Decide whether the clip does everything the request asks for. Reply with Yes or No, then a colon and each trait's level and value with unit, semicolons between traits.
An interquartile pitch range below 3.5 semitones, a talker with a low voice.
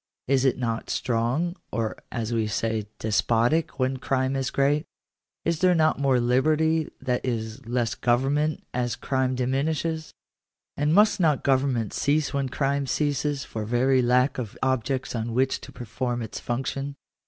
Yes: average, 3.1 semitones; low, 130 Hz